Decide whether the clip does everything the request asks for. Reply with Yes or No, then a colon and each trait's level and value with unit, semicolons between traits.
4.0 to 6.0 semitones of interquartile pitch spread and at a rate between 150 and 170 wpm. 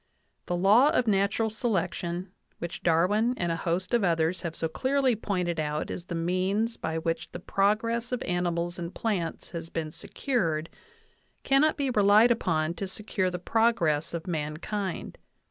Yes: average, 4.9 semitones; average, 165 wpm